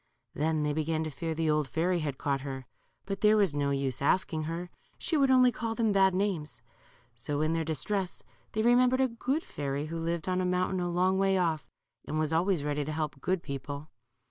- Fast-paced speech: Yes, fast, 215 wpm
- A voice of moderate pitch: Yes, medium, 165 Hz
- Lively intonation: No, average, 4.4 semitones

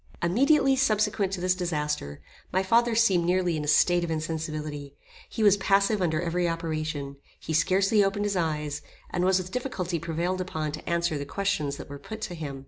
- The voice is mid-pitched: Yes, medium, 175 Hz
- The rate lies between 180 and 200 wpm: Yes, average, 190 wpm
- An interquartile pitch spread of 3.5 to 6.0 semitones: Yes, average, 4.2 semitones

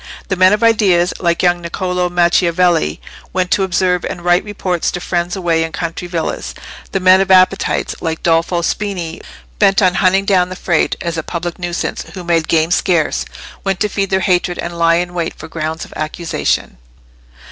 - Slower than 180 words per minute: No, average, 185 wpm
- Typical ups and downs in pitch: No, narrow, 1.6 semitones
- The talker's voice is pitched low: No, medium, 175 Hz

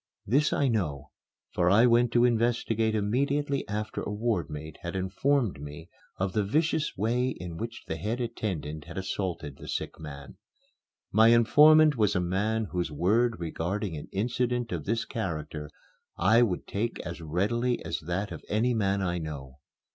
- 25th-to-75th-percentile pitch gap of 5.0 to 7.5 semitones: Yes, wide, 5.4 semitones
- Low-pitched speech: Yes, low, 105 Hz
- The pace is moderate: Yes, average, 165 wpm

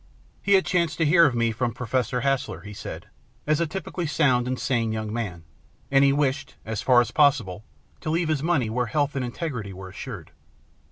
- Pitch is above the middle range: No, low, 130 Hz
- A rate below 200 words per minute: No, fast, 205 wpm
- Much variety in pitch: No, average, 4.9 semitones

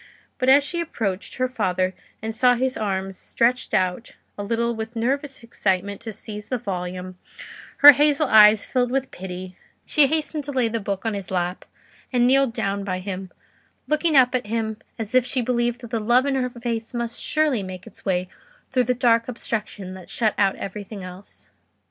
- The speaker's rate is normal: Yes, average, 190 wpm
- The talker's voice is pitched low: No, high, 230 Hz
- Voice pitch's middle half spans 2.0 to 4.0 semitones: No, average, 4.4 semitones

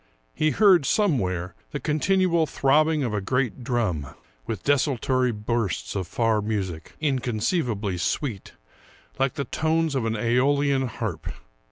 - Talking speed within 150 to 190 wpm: No, slow, 135 wpm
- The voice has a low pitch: Yes, low, 125 Hz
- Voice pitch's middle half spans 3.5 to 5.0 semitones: No, wide, 5.6 semitones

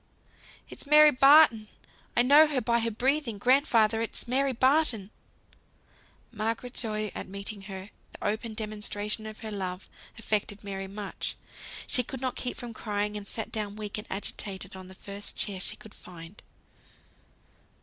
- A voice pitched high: Yes, high, 215 Hz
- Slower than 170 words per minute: Yes, average, 155 wpm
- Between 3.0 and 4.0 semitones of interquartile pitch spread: Yes, average, 3.4 semitones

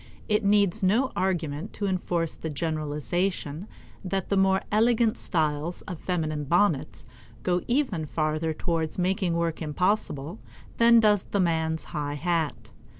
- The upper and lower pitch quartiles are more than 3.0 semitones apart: Yes, average, 4.1 semitones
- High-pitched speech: No, medium, 175 Hz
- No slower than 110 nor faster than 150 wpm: Yes, slow, 135 wpm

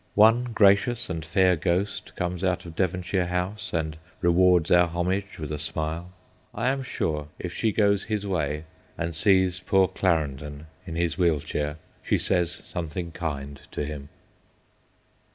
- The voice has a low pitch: Yes, very low, 90 Hz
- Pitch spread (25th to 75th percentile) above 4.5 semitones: No, average, 3.3 semitones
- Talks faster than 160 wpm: No, average, 155 wpm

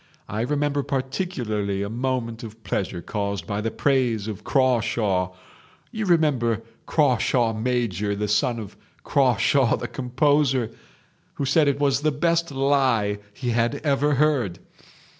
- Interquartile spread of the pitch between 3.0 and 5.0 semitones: Yes, average, 4.7 semitones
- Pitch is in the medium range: No, low, 125 Hz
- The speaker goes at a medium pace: No, slow, 125 wpm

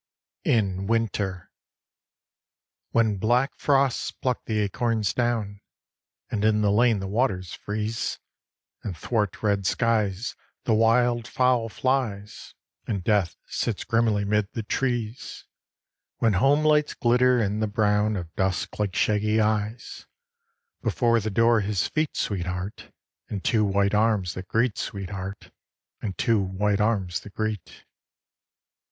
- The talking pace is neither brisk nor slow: No, slow, 130 wpm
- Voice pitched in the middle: No, low, 105 Hz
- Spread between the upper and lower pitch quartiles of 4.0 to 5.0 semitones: No, narrow, 2.6 semitones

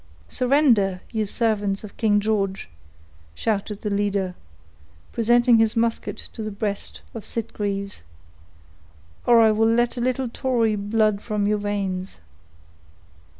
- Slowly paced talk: Yes, slow, 125 wpm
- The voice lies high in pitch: Yes, high, 215 Hz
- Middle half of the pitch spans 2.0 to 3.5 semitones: Yes, narrow, 2.4 semitones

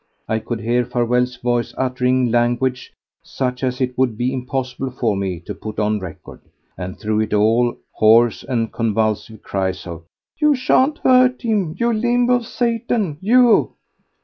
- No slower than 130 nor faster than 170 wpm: Yes, average, 150 wpm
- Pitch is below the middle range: Yes, low, 125 Hz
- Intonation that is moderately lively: No, wide, 7.7 semitones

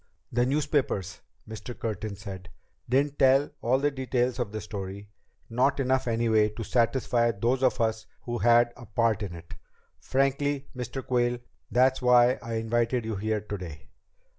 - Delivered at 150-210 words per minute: Yes, average, 155 wpm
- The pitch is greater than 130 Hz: No, low, 120 Hz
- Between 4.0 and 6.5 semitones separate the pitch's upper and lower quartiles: No, average, 3.1 semitones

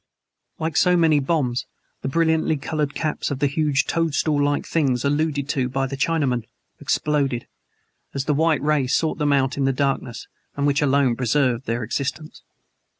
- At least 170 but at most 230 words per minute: No, average, 160 wpm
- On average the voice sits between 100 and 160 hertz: Yes, medium, 140 Hz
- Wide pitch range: No, narrow, 2.4 semitones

